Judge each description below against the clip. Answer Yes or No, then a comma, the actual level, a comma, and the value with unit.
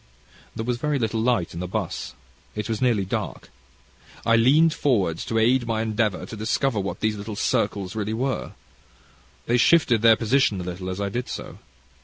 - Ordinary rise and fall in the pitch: Yes, average, 3.3 semitones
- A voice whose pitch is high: No, low, 110 Hz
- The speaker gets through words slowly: No, average, 180 wpm